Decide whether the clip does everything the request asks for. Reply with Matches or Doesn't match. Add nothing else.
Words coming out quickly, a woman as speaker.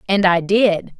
Doesn't match